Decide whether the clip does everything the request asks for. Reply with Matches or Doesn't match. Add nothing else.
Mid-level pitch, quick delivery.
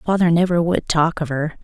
Matches